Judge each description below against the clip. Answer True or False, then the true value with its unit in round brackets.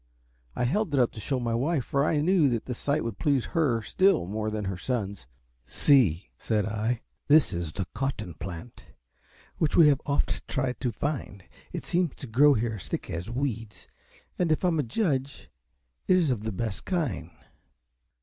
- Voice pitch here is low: True (125 Hz)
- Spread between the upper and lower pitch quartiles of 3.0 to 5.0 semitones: False (5.4 semitones)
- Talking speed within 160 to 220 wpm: True (190 wpm)